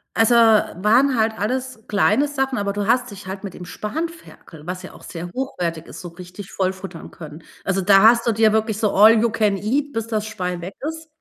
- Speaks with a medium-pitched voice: No, high, 215 Hz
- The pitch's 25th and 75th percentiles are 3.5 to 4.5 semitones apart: Yes, average, 3.8 semitones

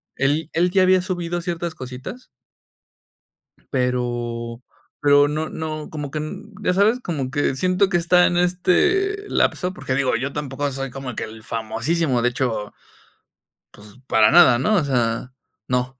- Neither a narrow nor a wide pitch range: No, wide, 6.0 semitones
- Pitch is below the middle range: No, medium, 145 Hz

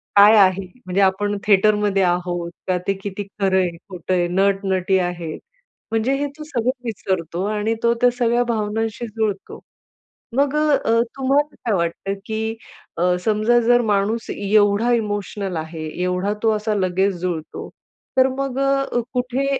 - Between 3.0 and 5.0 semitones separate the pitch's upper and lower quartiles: Yes, average, 3.8 semitones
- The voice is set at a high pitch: Yes, high, 205 Hz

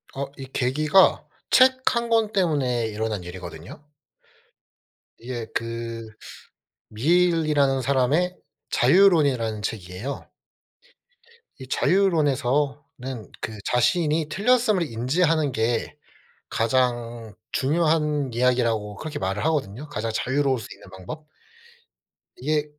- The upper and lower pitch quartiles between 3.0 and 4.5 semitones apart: No, wide, 5.4 semitones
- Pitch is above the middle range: No, low, 135 Hz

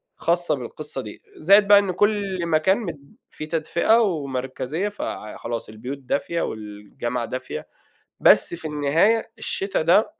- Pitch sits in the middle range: Yes, medium, 160 Hz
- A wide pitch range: Yes, wide, 7.0 semitones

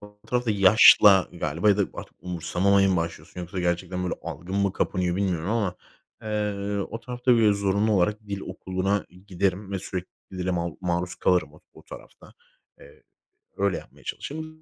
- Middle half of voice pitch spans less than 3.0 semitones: Yes, narrow, 2.6 semitones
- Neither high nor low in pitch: No, very low, 95 Hz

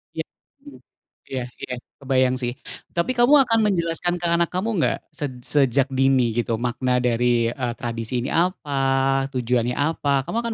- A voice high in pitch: No, low, 135 Hz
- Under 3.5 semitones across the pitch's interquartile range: No, average, 5.2 semitones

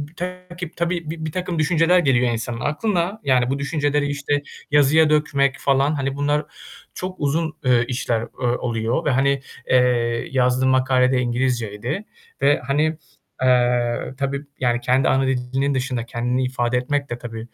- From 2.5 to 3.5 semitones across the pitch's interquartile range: Yes, average, 3.2 semitones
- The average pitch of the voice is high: No, low, 135 Hz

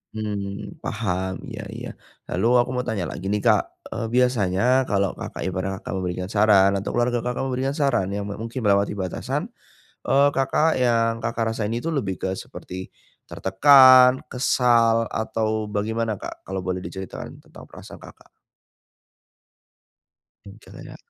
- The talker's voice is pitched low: Yes, low, 110 Hz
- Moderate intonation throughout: Yes, average, 4.1 semitones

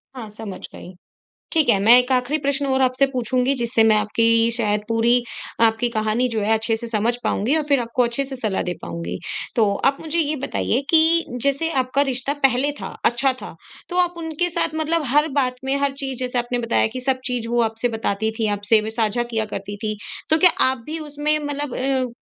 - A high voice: Yes, very high, 250 Hz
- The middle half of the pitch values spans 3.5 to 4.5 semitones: Yes, average, 4.0 semitones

